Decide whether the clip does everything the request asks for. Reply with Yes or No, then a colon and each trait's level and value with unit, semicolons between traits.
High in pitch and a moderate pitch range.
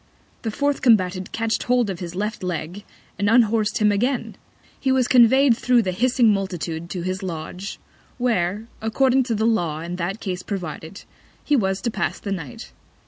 Yes: high, 205 Hz; average, 4.6 semitones